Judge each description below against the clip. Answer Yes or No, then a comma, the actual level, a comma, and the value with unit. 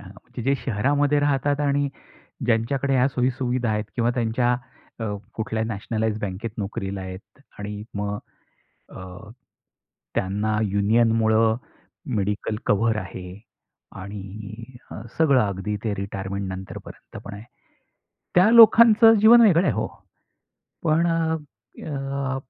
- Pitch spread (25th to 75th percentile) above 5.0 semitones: Yes, wide, 5.4 semitones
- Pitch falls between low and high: No, low, 115 Hz